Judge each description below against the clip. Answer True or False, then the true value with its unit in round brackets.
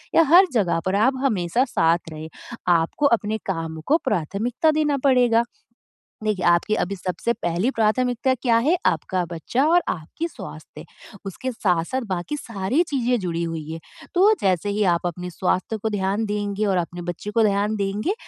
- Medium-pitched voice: False (205 Hz)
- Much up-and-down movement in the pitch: True (5.9 semitones)